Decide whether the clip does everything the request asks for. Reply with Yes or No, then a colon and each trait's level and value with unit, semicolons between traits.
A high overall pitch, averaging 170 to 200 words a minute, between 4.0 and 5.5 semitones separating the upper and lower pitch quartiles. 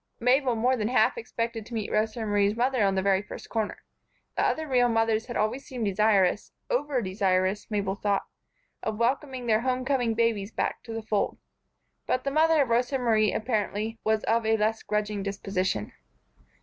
No: high, 225 Hz; average, 180 wpm; average, 3.2 semitones